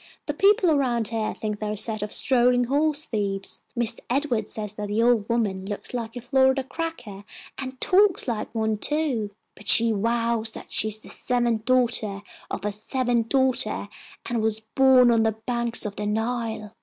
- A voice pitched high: Yes, high, 230 Hz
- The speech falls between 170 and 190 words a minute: Yes, average, 185 wpm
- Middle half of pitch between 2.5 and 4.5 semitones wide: Yes, average, 3.1 semitones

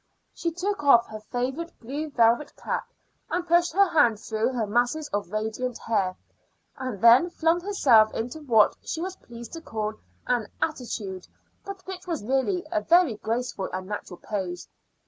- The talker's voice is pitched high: Yes, high, 245 Hz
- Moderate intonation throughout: No, wide, 7.2 semitones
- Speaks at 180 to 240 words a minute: No, average, 165 wpm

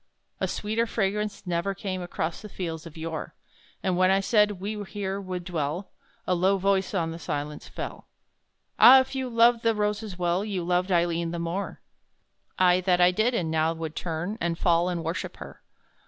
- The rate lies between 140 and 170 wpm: No, average, 185 wpm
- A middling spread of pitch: Yes, average, 3.3 semitones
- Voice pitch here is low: No, medium, 185 Hz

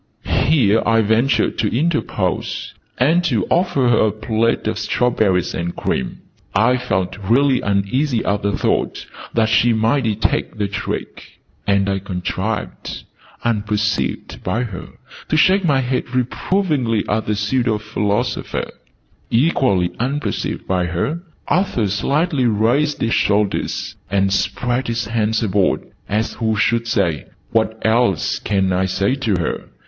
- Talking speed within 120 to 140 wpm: Yes, slow, 135 wpm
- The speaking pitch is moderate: No, low, 110 Hz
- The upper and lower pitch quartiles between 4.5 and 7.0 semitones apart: No, average, 3.9 semitones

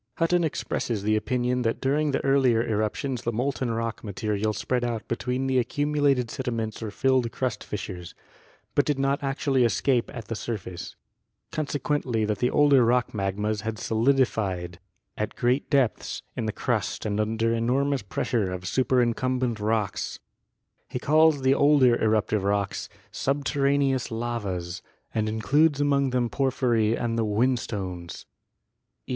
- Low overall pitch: Yes, low, 120 Hz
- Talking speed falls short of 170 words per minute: Yes, average, 150 wpm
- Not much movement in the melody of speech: No, average, 3.9 semitones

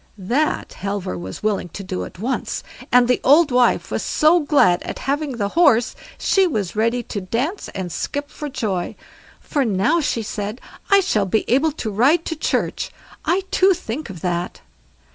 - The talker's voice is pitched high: Yes, high, 240 Hz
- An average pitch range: No, wide, 7.1 semitones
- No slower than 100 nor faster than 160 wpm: No, average, 180 wpm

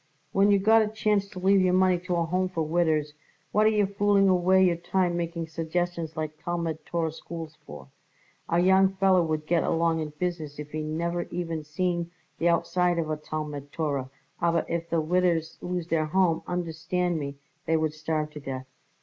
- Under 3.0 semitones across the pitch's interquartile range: Yes, narrow, 2.6 semitones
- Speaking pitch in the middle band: Yes, medium, 170 Hz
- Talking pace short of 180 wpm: No, average, 190 wpm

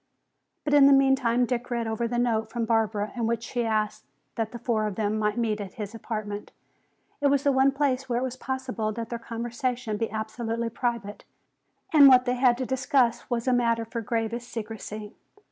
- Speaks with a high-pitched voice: Yes, high, 235 Hz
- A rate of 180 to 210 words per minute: Yes, average, 200 wpm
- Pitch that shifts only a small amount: Yes, narrow, 2.3 semitones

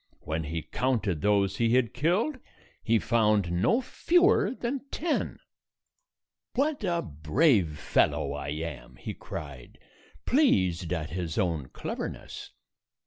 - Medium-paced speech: No, slow, 120 wpm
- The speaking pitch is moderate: No, low, 100 Hz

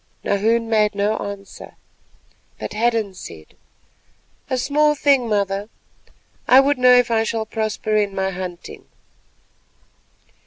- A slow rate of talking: Yes, slow, 120 wpm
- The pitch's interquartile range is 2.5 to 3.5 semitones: Yes, average, 3.2 semitones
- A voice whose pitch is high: Yes, high, 215 Hz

